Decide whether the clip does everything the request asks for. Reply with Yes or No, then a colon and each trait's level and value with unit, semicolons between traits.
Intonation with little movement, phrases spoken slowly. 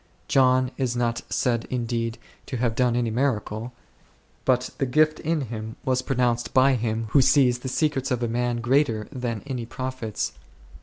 No: narrow, 2.0 semitones; average, 165 wpm